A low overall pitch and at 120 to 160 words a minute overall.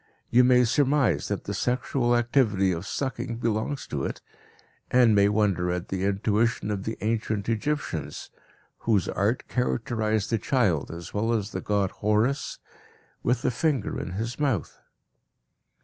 Yes: low, 110 Hz; average, 150 wpm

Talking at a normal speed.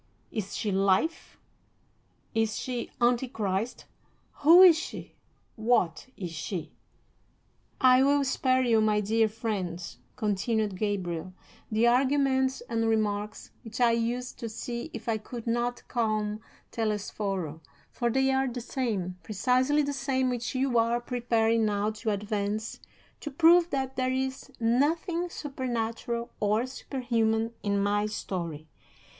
No: slow, 130 wpm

